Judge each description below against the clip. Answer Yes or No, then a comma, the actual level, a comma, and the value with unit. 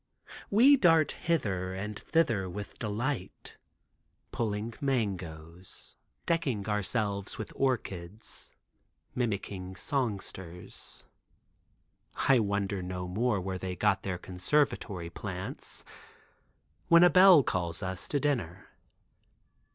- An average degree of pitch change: No, wide, 5.8 semitones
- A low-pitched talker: Yes, low, 100 Hz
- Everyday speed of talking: No, slow, 95 wpm